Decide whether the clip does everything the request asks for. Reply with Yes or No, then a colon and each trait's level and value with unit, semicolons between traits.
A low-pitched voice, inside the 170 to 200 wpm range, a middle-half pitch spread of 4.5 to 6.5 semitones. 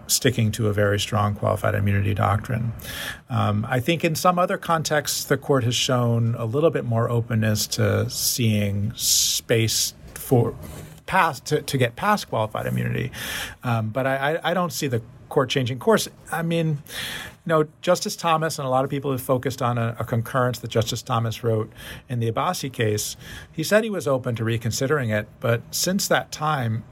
Yes: low, 125 Hz; average, 185 wpm; average, 5.1 semitones